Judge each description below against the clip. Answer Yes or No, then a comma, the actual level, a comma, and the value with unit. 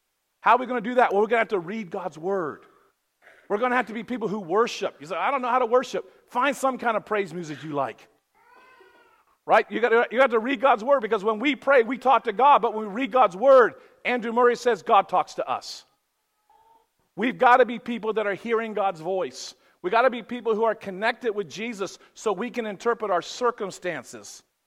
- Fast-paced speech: Yes, fast, 230 wpm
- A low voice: No, high, 235 Hz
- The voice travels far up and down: No, average, 3.4 semitones